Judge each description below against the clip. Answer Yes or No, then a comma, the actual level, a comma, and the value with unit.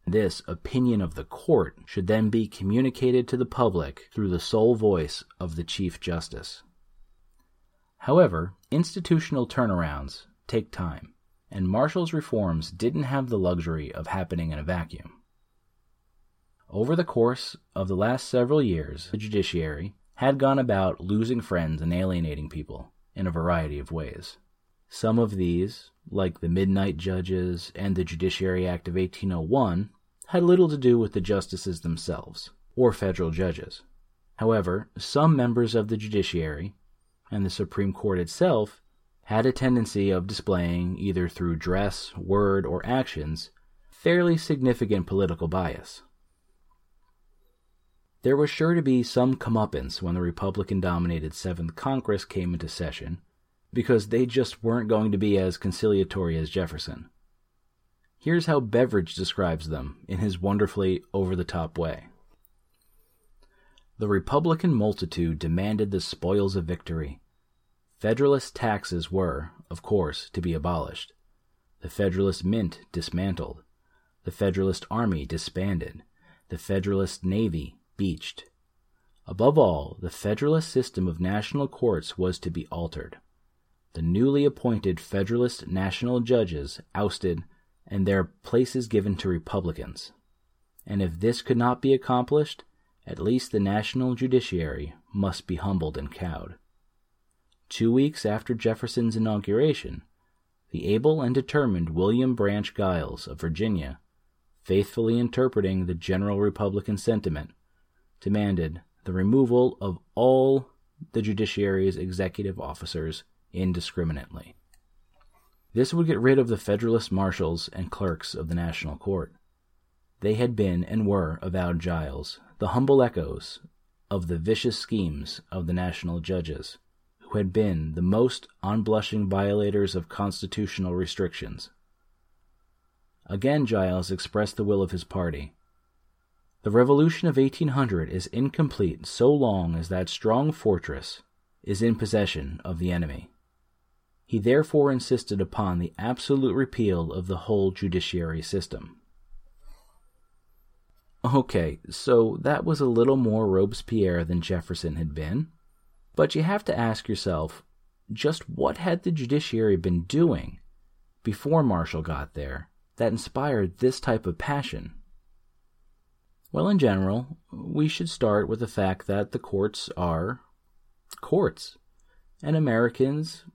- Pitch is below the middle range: Yes, very low, 95 Hz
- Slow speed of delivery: Yes, slow, 130 wpm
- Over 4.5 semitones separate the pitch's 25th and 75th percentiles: Yes, average, 5.2 semitones